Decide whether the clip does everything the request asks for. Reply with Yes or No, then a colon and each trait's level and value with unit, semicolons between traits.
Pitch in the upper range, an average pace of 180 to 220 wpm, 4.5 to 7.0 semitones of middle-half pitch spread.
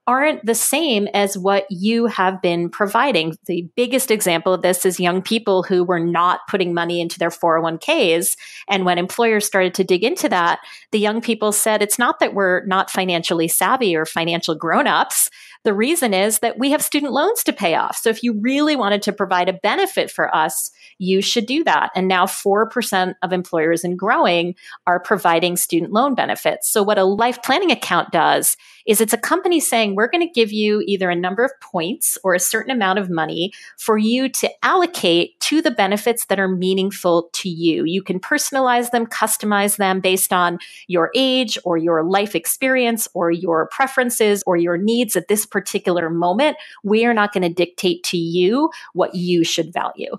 Yes: high, 200 Hz; average, 190 wpm; average, 4.8 semitones